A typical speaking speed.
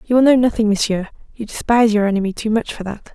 No: fast, 250 wpm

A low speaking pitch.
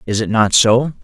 Yes: low, 115 Hz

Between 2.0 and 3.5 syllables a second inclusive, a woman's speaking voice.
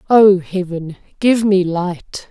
Yes: 3.2 syllables/s; female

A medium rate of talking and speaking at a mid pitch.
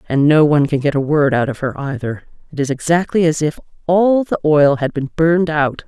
No: fast, 235 wpm; medium, 150 Hz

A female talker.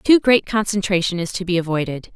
Yes: female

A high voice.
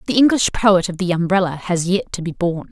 No: medium, 180 Hz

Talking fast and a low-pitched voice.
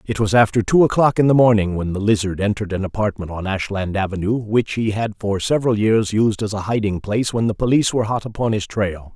Yes: fast, 235 wpm; low, 105 Hz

